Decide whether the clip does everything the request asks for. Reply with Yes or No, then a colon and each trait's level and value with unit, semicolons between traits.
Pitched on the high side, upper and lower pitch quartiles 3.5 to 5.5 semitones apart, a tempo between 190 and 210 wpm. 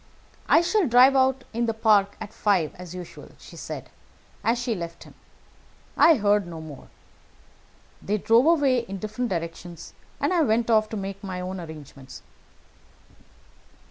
No: high, 210 Hz; average, 5.1 semitones; average, 155 wpm